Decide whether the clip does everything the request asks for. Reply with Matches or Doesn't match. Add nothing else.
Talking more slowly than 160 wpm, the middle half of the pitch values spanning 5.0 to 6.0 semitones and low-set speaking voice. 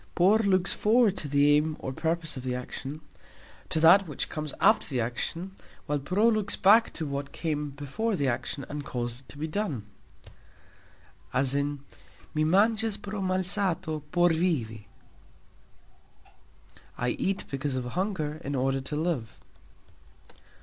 Doesn't match